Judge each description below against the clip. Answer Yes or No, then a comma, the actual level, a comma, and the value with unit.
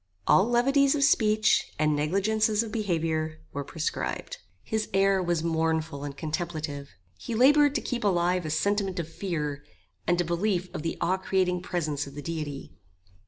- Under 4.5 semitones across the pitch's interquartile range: No, average, 5.1 semitones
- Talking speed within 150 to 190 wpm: Yes, average, 165 wpm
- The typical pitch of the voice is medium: Yes, medium, 175 Hz